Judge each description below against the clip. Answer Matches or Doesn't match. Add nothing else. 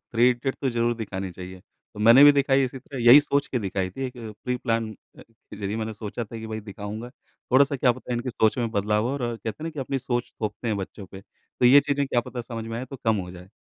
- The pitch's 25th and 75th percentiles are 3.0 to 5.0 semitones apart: Matches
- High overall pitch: Doesn't match